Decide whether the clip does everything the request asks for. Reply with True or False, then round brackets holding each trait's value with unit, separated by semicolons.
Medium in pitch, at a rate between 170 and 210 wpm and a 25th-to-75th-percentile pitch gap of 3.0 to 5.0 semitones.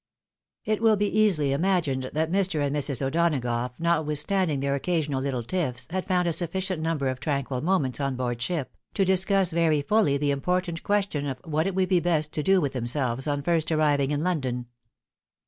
True (155 Hz; 190 wpm; 4.7 semitones)